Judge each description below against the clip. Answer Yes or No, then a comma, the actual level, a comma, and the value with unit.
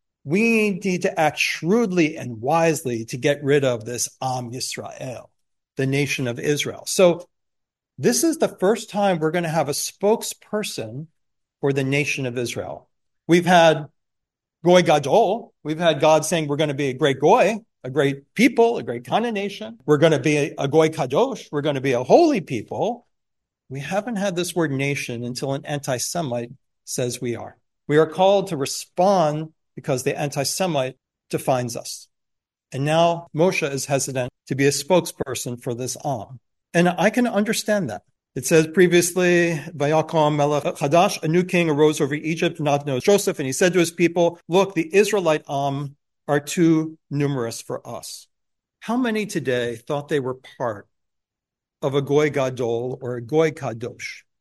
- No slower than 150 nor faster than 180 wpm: Yes, average, 170 wpm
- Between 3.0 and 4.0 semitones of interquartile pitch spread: No, average, 4.7 semitones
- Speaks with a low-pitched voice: No, medium, 150 Hz